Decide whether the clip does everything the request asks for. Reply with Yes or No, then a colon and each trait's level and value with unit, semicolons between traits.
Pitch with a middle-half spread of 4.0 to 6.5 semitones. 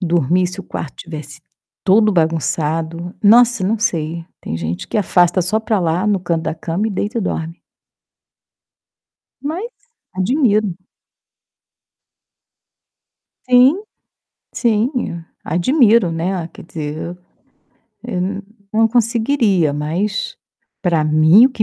Yes: average, 5.1 semitones